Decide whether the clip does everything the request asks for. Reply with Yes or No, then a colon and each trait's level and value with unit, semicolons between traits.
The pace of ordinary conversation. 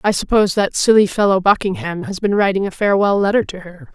No: fast, 215 wpm